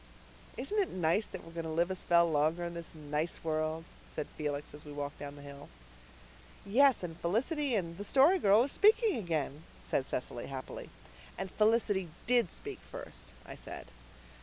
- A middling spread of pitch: No, wide, 6.2 semitones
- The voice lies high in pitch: No, medium, 170 Hz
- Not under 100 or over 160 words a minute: No, average, 180 wpm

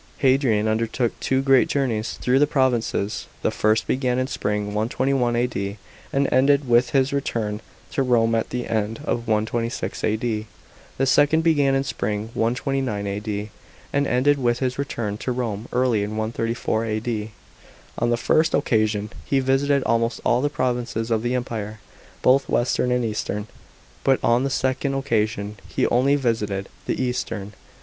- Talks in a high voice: No, low, 120 Hz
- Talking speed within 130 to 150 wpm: No, average, 160 wpm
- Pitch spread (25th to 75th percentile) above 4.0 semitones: No, average, 3.4 semitones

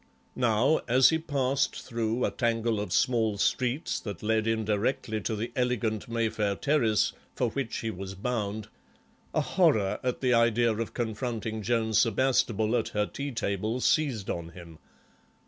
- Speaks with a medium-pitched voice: No, low, 115 Hz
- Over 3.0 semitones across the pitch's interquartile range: No, average, 2.7 semitones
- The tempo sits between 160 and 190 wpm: No, average, 150 wpm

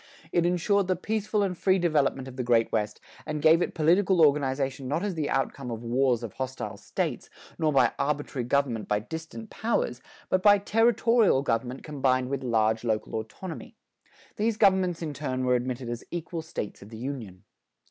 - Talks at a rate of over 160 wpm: Yes, average, 180 wpm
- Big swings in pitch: Yes, wide, 6.2 semitones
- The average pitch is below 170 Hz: Yes, medium, 140 Hz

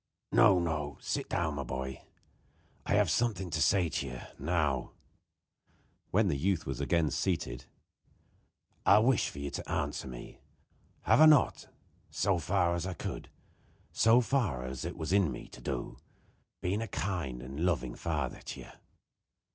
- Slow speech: No, average, 155 wpm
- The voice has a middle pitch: No, very low, 85 Hz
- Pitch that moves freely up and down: Yes, wide, 6.0 semitones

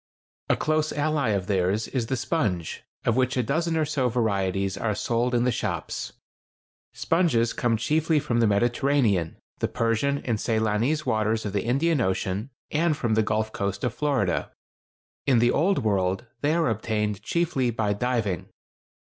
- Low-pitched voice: Yes, low, 115 Hz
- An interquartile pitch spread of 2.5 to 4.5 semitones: No, average, 5.1 semitones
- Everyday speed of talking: Yes, average, 165 wpm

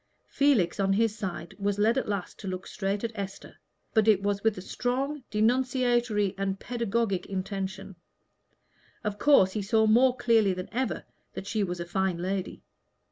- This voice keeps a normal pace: Yes, average, 170 wpm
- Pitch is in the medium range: No, high, 205 Hz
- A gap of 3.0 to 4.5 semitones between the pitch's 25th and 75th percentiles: Yes, average, 3.3 semitones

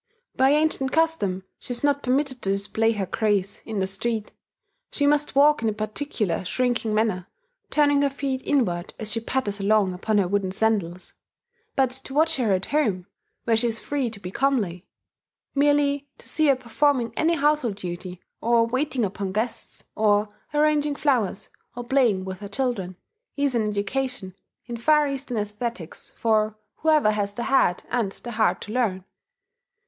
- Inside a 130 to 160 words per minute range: No, average, 170 wpm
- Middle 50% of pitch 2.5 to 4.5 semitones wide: No, wide, 5.4 semitones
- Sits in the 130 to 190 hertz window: No, high, 230 Hz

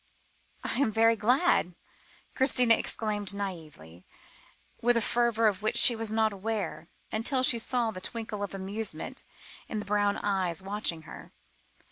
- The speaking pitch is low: No, high, 215 Hz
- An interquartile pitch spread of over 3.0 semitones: No, average, 2.7 semitones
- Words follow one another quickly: No, average, 145 wpm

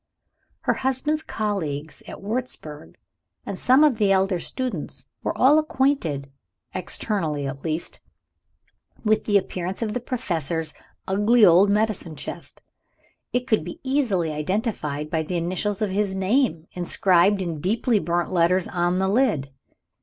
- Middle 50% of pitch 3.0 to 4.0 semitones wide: No, average, 5.1 semitones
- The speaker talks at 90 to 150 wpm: Yes, average, 140 wpm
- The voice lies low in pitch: No, high, 190 Hz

